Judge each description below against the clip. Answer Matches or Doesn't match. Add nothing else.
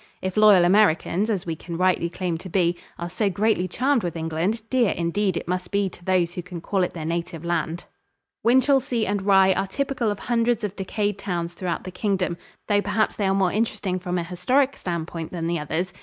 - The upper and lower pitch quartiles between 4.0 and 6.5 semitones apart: Doesn't match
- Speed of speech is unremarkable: Doesn't match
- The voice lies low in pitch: Doesn't match